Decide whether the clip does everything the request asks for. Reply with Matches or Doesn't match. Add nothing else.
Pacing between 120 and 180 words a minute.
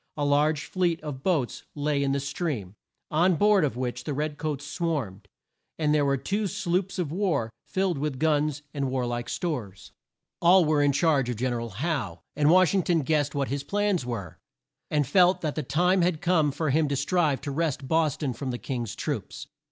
Doesn't match